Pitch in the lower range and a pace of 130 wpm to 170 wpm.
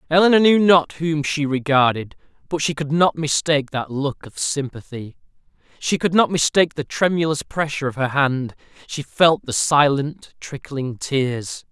No: medium, 145 Hz; average, 160 wpm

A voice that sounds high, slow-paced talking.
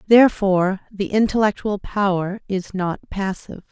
Yes: high, 195 Hz; slow, 115 wpm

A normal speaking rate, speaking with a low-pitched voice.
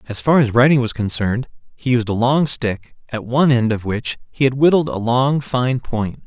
No: fast, 220 wpm; low, 125 Hz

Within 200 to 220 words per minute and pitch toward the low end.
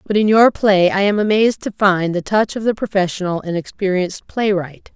No: fast, 205 wpm; high, 195 Hz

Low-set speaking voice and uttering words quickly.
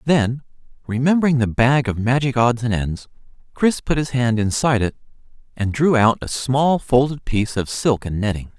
No: low, 125 Hz; average, 180 wpm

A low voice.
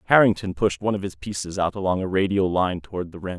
Yes: very low, 95 Hz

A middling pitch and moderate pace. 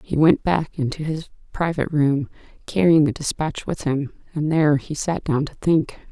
Yes: medium, 150 Hz; average, 185 wpm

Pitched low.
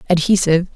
No: medium, 170 Hz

